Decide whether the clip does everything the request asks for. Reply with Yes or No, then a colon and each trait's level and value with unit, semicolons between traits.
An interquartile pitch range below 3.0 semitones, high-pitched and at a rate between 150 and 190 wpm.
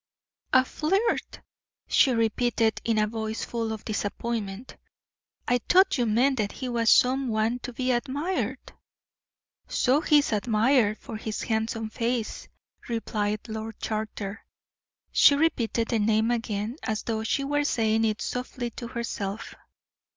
No: narrow, 2.6 semitones; high, 230 Hz; average, 140 wpm